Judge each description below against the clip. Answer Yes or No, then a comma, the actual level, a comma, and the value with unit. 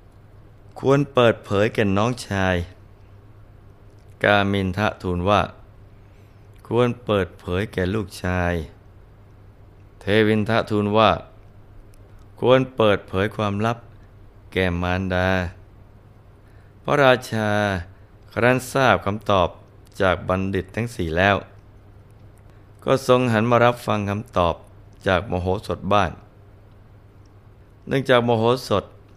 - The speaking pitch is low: Yes, low, 100 Hz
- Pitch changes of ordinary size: No, narrow, 1.3 semitones